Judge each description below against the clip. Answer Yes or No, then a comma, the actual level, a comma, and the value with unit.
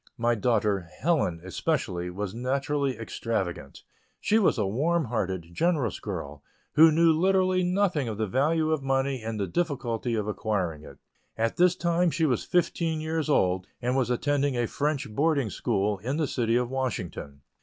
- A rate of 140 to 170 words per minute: Yes, average, 165 wpm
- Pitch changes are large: Yes, wide, 6.9 semitones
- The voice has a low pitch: Yes, low, 130 Hz